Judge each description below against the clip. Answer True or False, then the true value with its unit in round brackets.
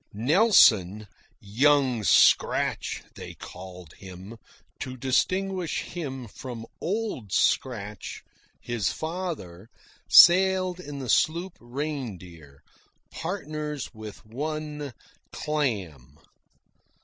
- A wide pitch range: True (7.3 semitones)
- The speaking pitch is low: True (130 Hz)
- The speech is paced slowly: True (80 wpm)